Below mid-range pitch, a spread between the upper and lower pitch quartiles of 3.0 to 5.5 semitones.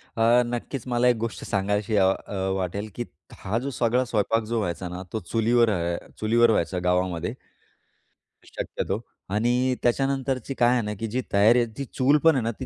Yes: low, 115 Hz; average, 3.3 semitones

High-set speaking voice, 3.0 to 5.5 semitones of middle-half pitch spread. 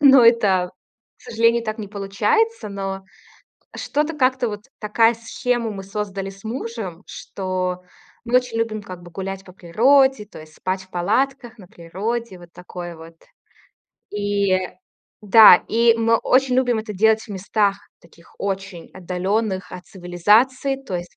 Yes: high, 205 Hz; average, 3.9 semitones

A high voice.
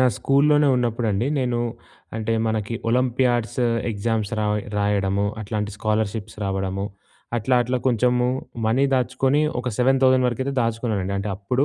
No: low, 115 Hz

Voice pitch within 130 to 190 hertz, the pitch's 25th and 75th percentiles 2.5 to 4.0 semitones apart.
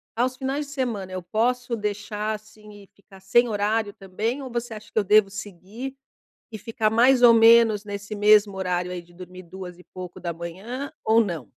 No: high, 210 Hz; average, 3.5 semitones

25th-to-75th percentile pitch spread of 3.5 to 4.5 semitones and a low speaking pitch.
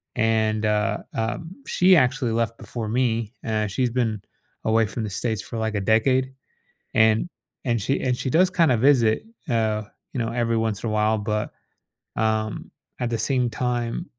No: narrow, 2.4 semitones; low, 115 Hz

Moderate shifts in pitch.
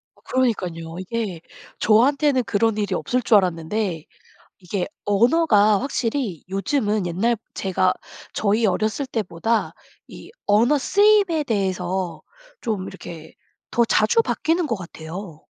Yes: average, 4.8 semitones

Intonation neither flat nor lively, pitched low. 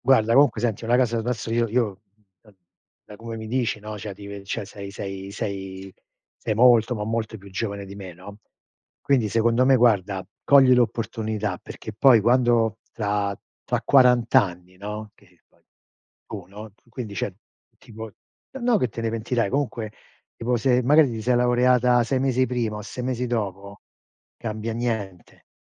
Yes: average, 3.3 semitones; low, 110 Hz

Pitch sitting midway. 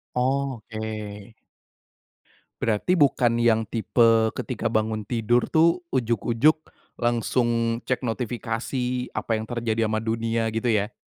No: low, 115 Hz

